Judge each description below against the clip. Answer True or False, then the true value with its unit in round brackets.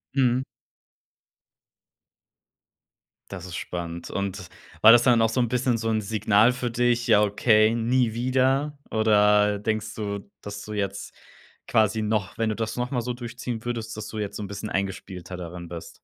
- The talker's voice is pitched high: False (110 Hz)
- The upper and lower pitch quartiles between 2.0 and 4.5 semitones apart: True (2.9 semitones)